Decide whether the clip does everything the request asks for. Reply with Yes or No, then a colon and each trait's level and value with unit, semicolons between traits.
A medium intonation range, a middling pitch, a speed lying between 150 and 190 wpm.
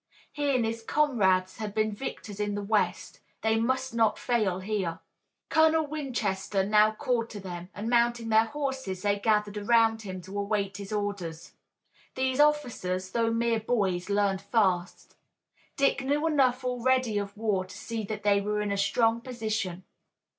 No: average, 3.2 semitones; high, 215 Hz; average, 160 wpm